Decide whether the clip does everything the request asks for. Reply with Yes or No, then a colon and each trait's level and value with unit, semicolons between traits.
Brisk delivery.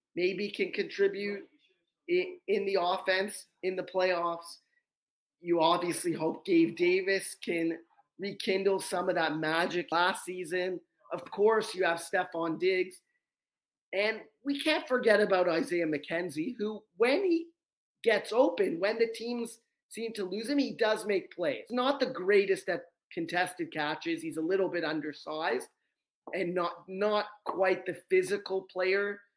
No: average, 145 wpm